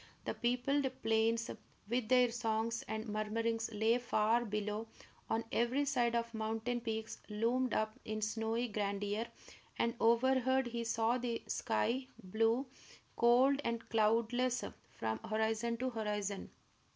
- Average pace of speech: No, slow, 125 wpm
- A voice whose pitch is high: Yes, high, 230 Hz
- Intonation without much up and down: Yes, narrow, 1.9 semitones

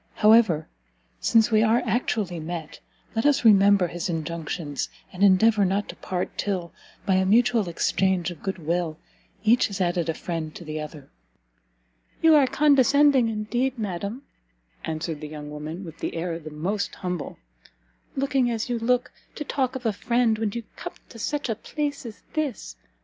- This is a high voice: Yes, high, 200 Hz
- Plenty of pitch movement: Yes, wide, 5.8 semitones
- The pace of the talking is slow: No, average, 170 wpm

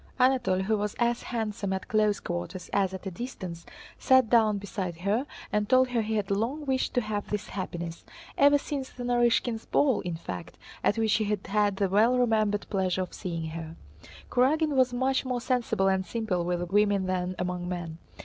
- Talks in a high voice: Yes, high, 210 Hz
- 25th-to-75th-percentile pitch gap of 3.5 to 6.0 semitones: Yes, average, 4.7 semitones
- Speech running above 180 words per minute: Yes, average, 190 wpm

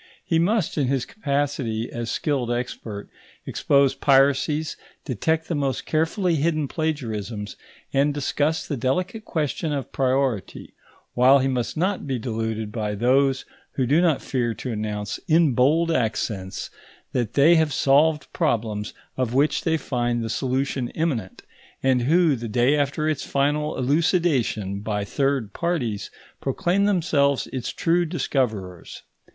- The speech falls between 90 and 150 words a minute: Yes, average, 140 wpm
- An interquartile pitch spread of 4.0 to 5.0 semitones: Yes, average, 4.7 semitones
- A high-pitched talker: No, low, 135 Hz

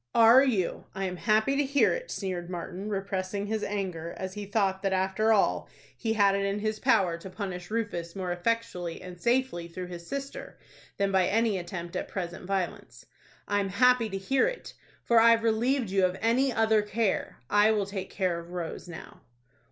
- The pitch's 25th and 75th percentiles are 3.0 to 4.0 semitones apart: Yes, average, 3.5 semitones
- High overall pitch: Yes, high, 200 Hz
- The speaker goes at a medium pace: Yes, average, 190 wpm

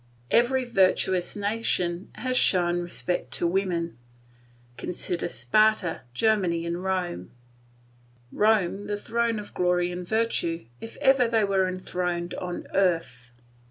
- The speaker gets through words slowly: Yes, slow, 120 wpm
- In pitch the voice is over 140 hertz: Yes, medium, 185 Hz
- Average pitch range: Yes, average, 3.7 semitones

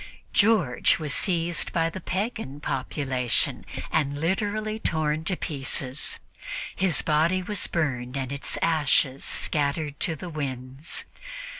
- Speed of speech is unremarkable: No, slow, 120 wpm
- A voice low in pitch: No, medium, 155 Hz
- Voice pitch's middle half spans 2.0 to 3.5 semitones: No, average, 4.4 semitones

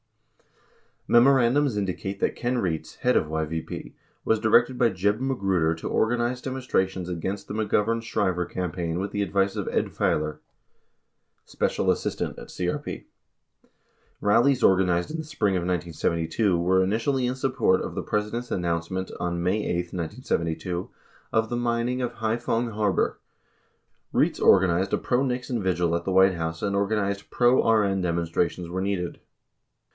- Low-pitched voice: Yes, low, 100 Hz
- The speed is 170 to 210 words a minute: No, average, 155 wpm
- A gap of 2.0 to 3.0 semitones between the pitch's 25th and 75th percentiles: No, average, 5.0 semitones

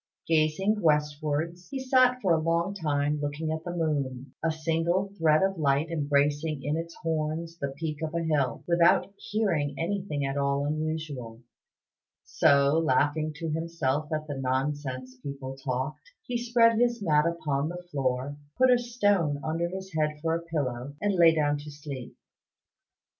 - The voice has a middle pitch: Yes, medium, 155 Hz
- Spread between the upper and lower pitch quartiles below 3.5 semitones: Yes, average, 2.8 semitones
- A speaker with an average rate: Yes, average, 160 wpm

